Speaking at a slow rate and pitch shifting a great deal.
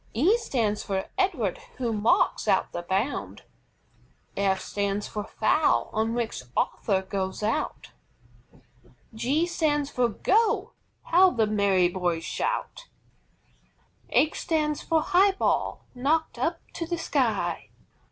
Yes: slow, 125 wpm; wide, 8.5 semitones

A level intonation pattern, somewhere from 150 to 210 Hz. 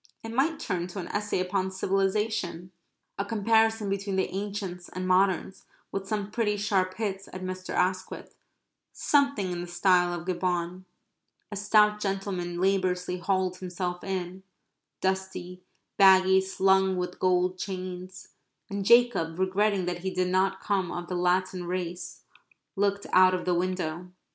Yes: narrow, 1.6 semitones; medium, 185 Hz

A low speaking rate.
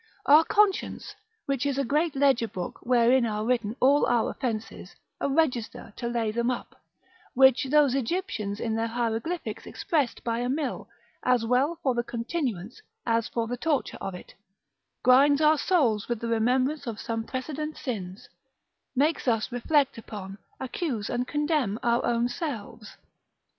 No: average, 155 wpm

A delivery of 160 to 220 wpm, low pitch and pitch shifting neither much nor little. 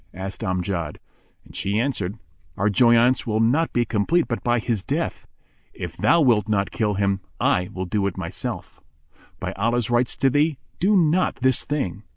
Yes: average, 185 wpm; low, 115 Hz; average, 4.7 semitones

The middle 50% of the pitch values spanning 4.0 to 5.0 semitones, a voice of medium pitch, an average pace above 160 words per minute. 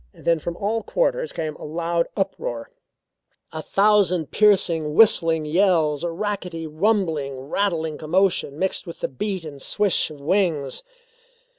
No: average, 4.4 semitones; medium, 170 Hz; slow, 135 wpm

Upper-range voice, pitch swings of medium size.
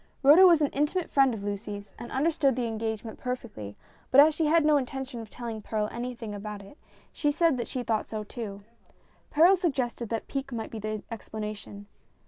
Yes: high, 240 Hz; average, 5.0 semitones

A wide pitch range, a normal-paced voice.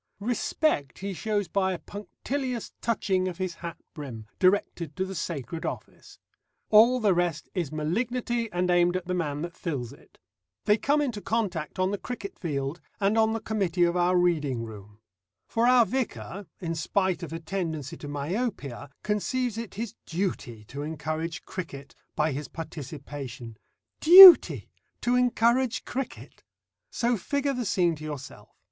Yes: wide, 6.3 semitones; average, 155 wpm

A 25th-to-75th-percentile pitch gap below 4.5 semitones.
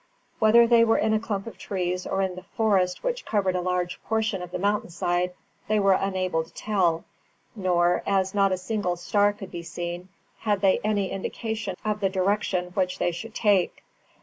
Yes: average, 2.7 semitones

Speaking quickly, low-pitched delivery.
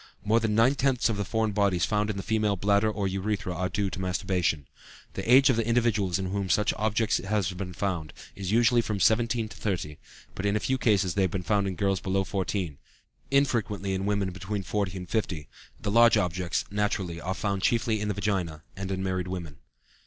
Yes: fast, 210 wpm; low, 100 Hz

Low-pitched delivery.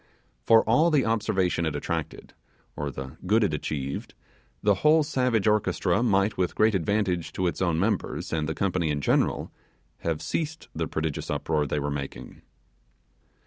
Yes: very low, 95 Hz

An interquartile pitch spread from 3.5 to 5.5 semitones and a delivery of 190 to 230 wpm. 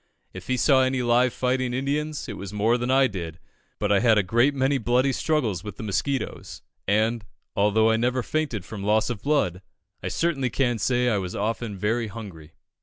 Yes: average, 3.9 semitones; average, 195 wpm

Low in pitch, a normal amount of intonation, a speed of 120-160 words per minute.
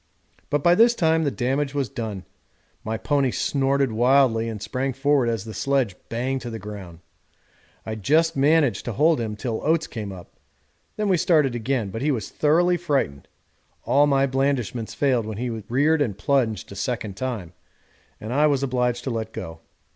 No: low, 130 Hz; average, 4.4 semitones; average, 180 wpm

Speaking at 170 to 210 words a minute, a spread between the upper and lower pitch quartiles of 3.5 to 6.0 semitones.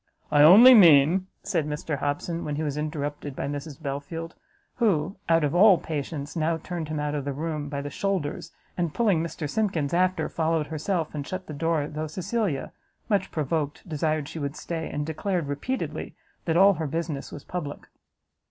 No: average, 180 wpm; average, 3.1 semitones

